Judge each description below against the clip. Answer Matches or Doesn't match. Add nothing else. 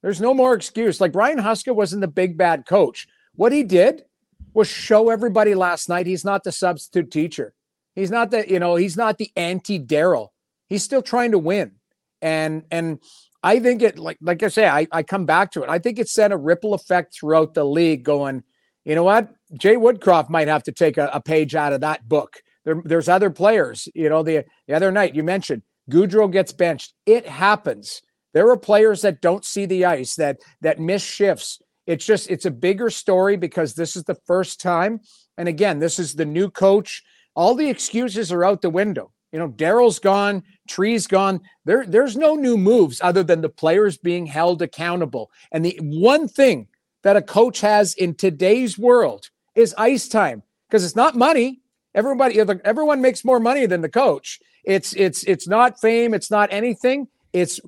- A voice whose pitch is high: Matches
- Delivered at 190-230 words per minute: Matches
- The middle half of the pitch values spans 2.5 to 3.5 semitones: Doesn't match